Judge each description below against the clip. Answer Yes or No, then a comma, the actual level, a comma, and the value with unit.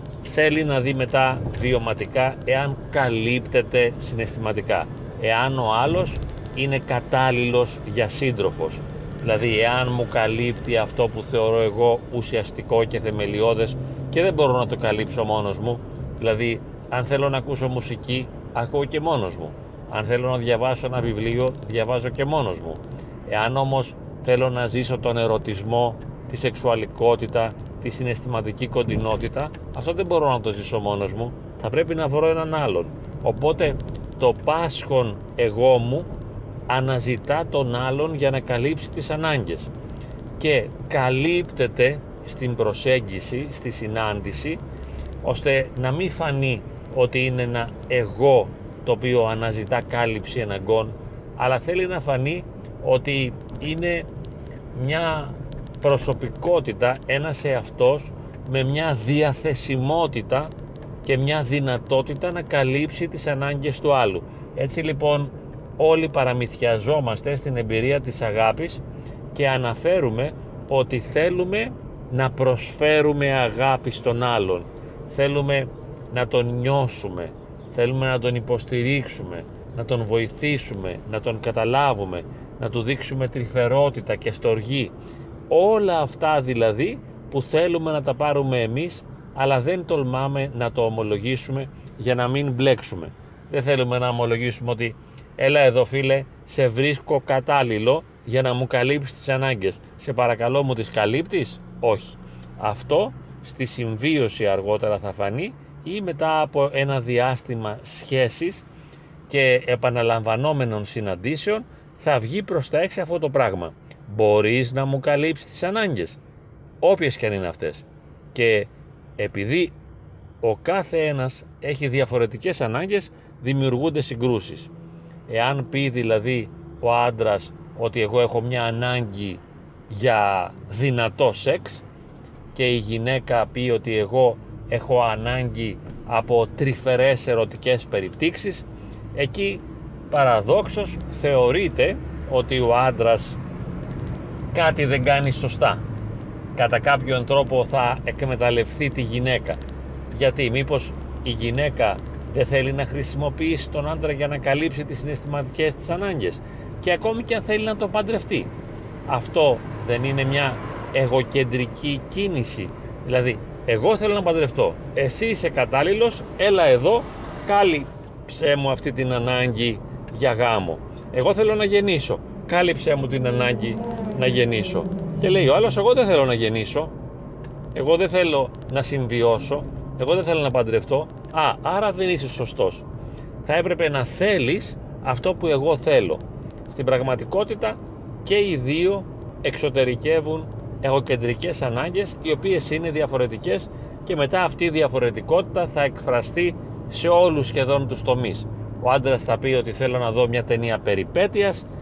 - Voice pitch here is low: Yes, low, 130 Hz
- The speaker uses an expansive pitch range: No, average, 3.7 semitones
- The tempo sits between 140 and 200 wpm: No, average, 125 wpm